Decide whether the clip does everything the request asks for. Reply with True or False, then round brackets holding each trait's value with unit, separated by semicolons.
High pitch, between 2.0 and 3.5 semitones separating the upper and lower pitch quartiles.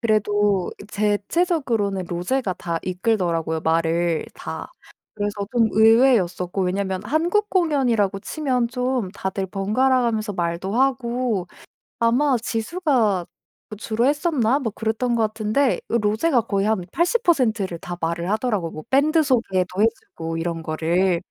False (215 Hz; 5.4 semitones)